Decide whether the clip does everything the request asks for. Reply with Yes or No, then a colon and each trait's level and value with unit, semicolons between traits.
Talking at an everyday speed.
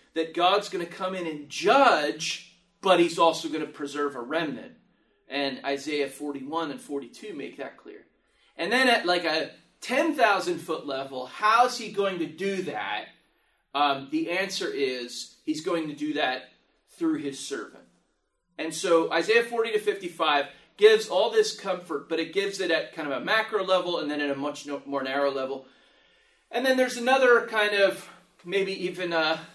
Yes: average, 180 wpm